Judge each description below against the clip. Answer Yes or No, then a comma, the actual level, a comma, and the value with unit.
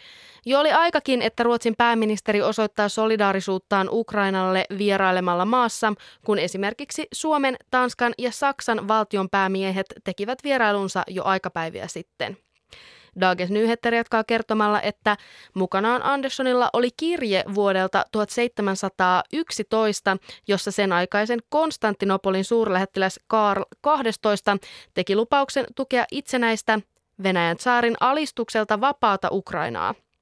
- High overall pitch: Yes, high, 215 Hz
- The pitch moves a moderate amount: Yes, average, 3.8 semitones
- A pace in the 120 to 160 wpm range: No, average, 100 wpm